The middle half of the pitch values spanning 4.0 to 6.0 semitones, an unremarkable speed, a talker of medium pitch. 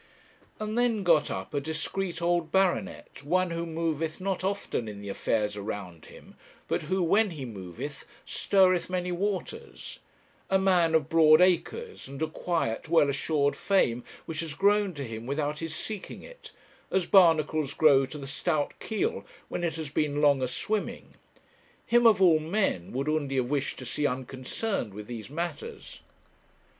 Yes: average, 5.1 semitones; average, 165 wpm; medium, 160 Hz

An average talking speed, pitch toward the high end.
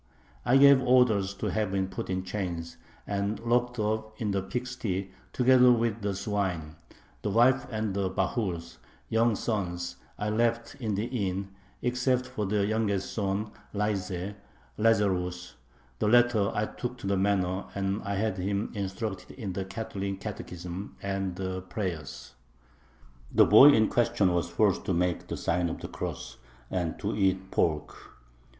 No: average, 155 wpm; low, 100 Hz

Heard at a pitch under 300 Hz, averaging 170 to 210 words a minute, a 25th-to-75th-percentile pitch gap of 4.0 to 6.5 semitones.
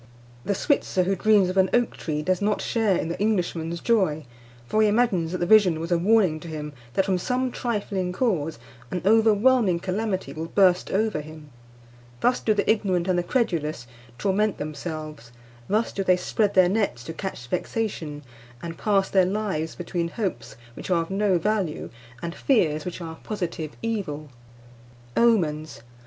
Yes: medium, 185 Hz; average, 175 wpm; average, 4.6 semitones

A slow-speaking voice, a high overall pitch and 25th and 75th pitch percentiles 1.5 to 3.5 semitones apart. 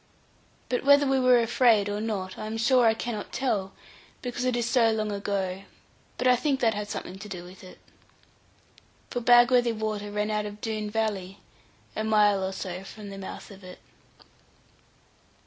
No: average, 180 wpm; high, 215 Hz; average, 3.2 semitones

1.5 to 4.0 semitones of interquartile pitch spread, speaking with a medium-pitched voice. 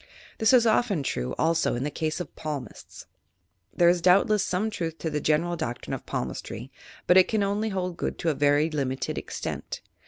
No: average, 4.8 semitones; medium, 170 Hz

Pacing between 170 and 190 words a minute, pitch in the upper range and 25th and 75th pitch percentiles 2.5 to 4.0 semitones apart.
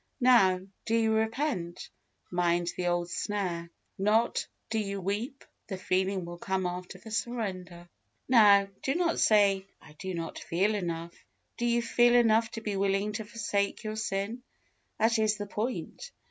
No: average, 160 wpm; high, 205 Hz; average, 3.6 semitones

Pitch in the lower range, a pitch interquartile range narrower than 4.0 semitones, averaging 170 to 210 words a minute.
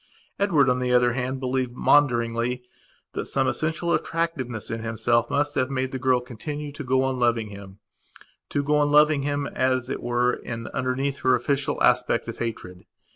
Yes: low, 130 Hz; average, 3.0 semitones; average, 175 wpm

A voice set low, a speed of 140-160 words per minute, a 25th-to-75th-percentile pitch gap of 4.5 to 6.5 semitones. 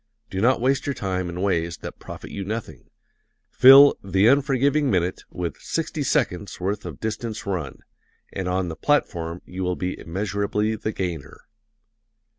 Yes: low, 100 Hz; average, 155 wpm; average, 4.8 semitones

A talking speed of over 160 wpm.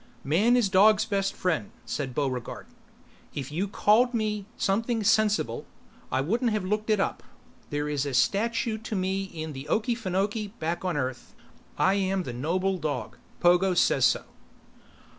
No: average, 155 wpm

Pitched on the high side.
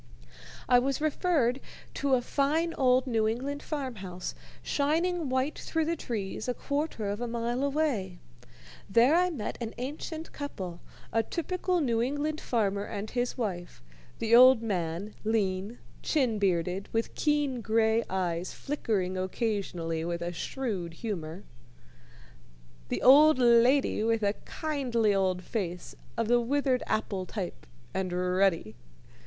Yes: high, 230 Hz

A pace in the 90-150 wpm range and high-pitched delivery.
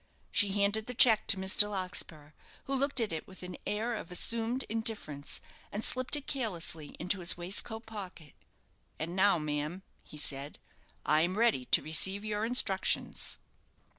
No: average, 160 wpm; high, 195 Hz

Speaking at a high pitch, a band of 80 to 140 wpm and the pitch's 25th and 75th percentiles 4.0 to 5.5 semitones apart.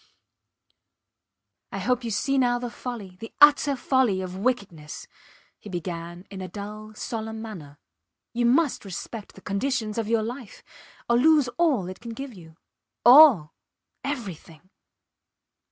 Yes: high, 220 Hz; slow, 135 wpm; average, 5.0 semitones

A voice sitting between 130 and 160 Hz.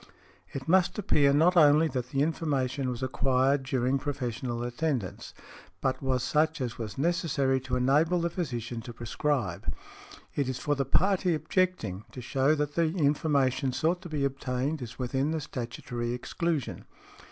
Yes: low, 135 Hz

